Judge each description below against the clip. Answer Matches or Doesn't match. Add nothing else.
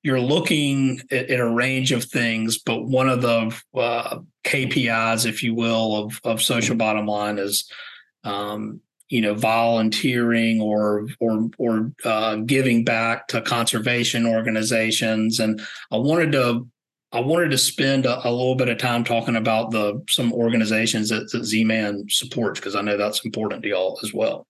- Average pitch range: Doesn't match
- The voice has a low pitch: Matches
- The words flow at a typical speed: Matches